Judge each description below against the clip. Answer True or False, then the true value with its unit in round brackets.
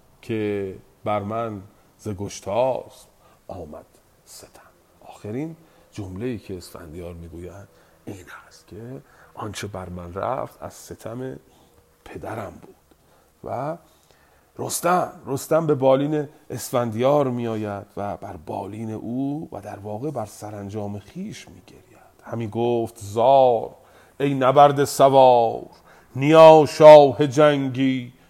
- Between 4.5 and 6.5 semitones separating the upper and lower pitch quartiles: True (5.2 semitones)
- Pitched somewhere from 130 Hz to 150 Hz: False (115 Hz)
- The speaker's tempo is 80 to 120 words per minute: True (110 wpm)